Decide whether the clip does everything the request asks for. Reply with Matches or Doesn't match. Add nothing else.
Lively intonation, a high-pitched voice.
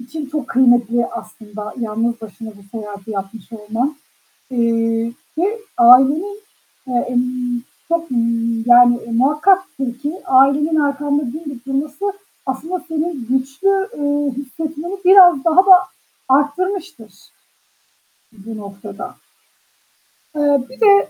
Doesn't match